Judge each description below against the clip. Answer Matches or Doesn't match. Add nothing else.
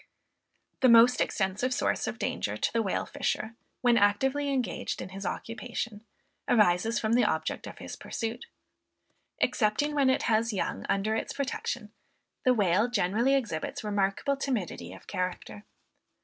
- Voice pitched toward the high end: Matches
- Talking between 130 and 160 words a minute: Matches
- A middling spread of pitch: Matches